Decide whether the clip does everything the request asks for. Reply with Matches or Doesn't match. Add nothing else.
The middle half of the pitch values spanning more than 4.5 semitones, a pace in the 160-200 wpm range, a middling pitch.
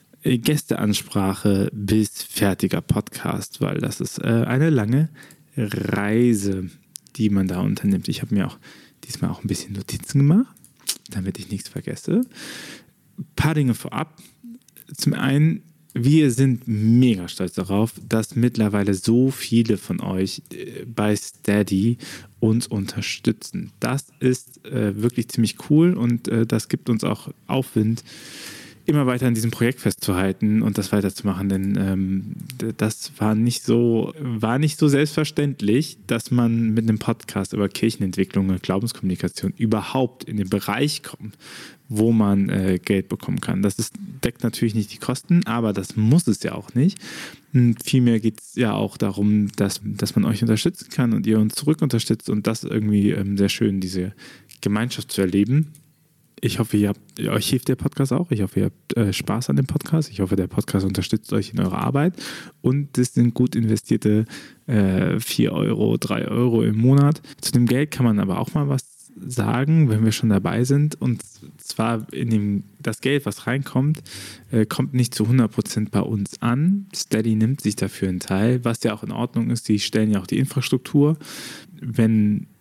Doesn't match